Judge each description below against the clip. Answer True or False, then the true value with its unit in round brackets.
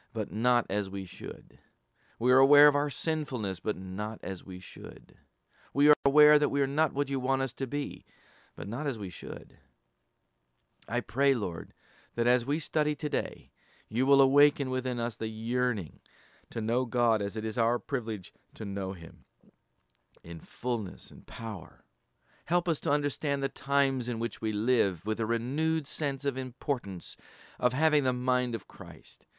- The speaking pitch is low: True (125 Hz)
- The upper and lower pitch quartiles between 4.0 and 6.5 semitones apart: True (4.7 semitones)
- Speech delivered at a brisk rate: False (175 wpm)